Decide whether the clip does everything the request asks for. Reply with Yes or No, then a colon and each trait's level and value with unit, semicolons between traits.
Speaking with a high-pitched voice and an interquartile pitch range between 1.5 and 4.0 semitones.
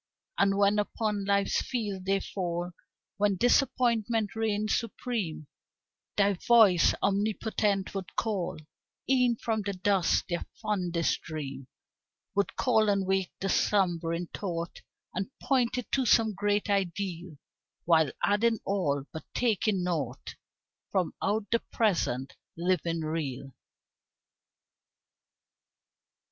Yes: high, 200 Hz; average, 3.7 semitones